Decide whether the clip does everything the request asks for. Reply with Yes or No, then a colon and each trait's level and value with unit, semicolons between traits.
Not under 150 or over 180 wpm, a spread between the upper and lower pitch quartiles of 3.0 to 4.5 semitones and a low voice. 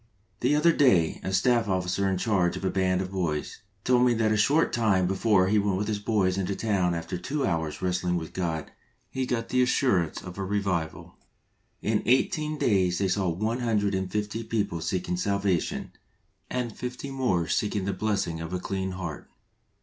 No: average, 195 wpm; average, 3.9 semitones; low, 100 Hz